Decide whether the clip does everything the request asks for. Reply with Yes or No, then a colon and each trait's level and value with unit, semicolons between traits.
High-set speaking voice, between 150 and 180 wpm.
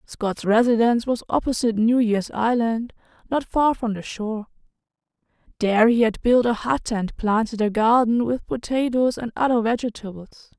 Yes: high, 230 Hz; average, 155 wpm